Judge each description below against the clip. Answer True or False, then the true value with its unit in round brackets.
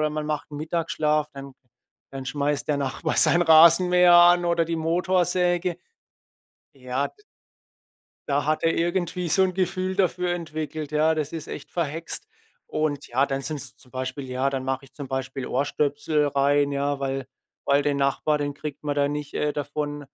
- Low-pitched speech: False (150 Hz)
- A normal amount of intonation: True (3.2 semitones)